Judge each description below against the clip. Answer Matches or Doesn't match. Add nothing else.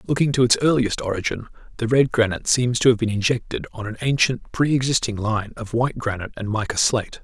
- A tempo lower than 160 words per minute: Doesn't match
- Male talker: Matches